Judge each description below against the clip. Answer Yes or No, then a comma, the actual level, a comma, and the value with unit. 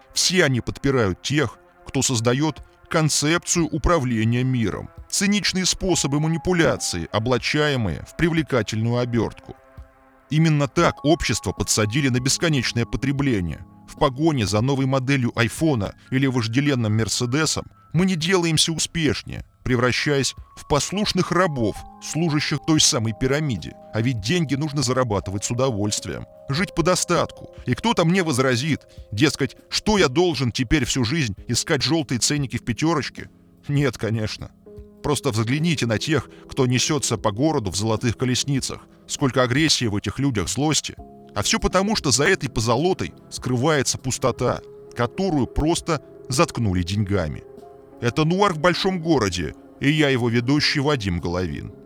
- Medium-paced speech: Yes, average, 130 wpm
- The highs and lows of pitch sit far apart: Yes, wide, 5.8 semitones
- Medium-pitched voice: No, low, 130 Hz